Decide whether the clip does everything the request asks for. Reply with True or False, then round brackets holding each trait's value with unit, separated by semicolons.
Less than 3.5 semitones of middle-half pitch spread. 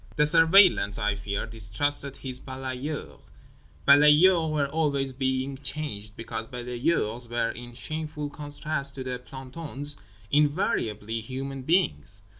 False (3.8 semitones)